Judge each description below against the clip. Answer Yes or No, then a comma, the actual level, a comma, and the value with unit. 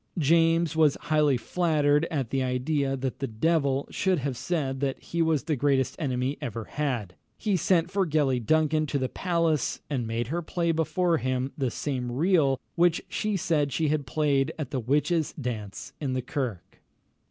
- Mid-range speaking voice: Yes, medium, 145 Hz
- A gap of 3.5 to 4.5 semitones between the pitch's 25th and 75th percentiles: Yes, average, 3.9 semitones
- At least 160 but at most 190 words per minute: Yes, average, 175 wpm